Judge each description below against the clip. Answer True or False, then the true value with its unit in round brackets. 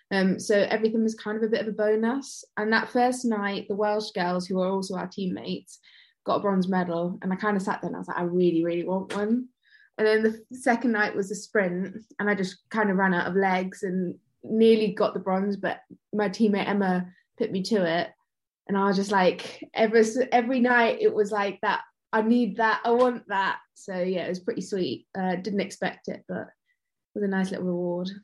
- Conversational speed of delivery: False (225 wpm)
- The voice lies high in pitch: True (205 Hz)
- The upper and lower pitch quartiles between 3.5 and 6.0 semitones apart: False (2.9 semitones)